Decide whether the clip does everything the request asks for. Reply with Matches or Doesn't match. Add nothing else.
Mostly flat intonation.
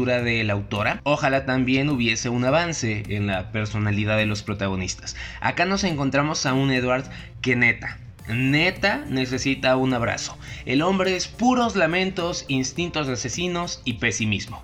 Doesn't match